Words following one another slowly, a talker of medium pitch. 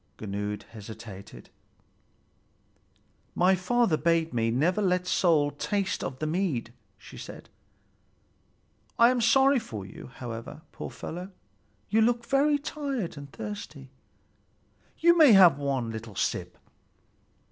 Yes: slow, 120 wpm; medium, 160 Hz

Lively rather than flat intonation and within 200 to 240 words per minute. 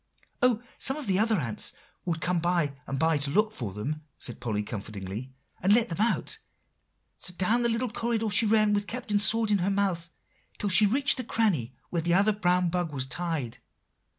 Yes: wide, 6.3 semitones; fast, 205 wpm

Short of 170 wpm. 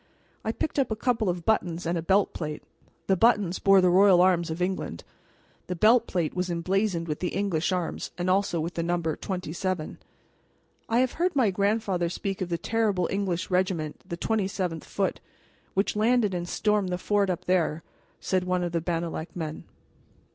No: average, 185 wpm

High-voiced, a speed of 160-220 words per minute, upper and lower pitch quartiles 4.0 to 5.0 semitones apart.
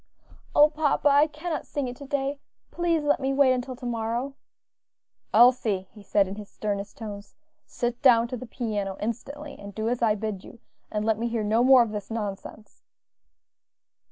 Yes: high, 235 Hz; average, 185 wpm; average, 4.4 semitones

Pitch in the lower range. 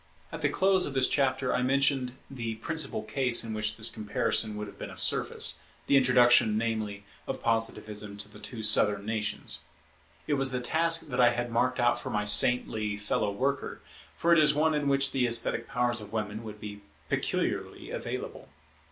Yes: low, 120 Hz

